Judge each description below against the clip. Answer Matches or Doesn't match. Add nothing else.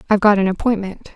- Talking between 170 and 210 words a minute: Matches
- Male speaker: Doesn't match